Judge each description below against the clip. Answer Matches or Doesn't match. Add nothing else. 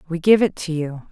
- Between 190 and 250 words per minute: Doesn't match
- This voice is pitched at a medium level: Matches